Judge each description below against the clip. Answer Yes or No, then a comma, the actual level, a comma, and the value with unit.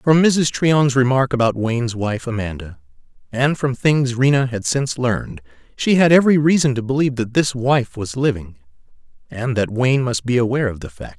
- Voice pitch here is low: Yes, low, 125 Hz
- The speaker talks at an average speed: Yes, average, 190 wpm